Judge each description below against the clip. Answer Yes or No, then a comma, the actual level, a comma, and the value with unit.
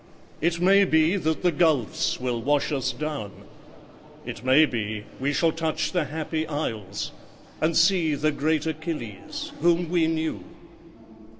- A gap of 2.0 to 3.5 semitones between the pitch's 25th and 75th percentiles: Yes, average, 2.8 semitones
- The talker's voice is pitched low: No, medium, 155 Hz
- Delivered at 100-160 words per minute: Yes, average, 140 wpm